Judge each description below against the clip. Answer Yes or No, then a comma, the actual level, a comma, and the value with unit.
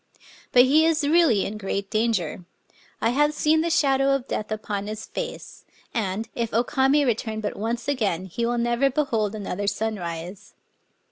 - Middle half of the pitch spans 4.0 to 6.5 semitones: Yes, average, 5.0 semitones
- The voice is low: No, high, 230 Hz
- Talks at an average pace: Yes, average, 165 wpm